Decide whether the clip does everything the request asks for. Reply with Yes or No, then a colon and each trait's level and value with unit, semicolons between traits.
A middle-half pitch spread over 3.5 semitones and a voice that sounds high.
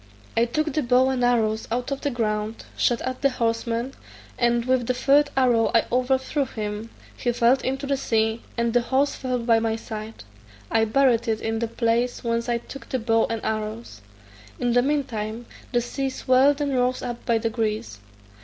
No: narrow, 2.4 semitones; high, 240 Hz